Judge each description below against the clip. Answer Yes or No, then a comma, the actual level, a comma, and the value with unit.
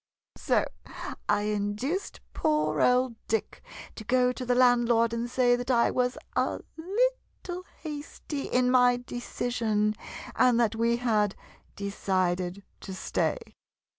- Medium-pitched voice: No, high, 245 Hz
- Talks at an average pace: No, slow, 125 wpm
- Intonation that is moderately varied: Yes, average, 3.1 semitones